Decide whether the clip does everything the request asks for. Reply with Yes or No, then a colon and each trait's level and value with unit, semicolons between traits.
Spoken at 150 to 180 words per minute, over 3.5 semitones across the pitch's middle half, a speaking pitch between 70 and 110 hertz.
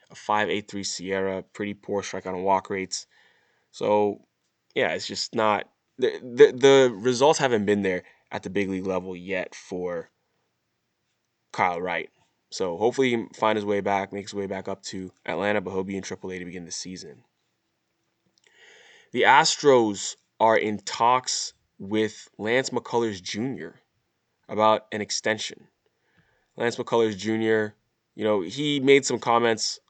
No: average, 155 wpm; average, 2.9 semitones; low, 105 Hz